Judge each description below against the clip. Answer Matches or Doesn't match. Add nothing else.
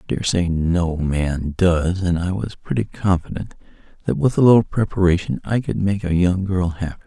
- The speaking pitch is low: Matches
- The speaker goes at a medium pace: Matches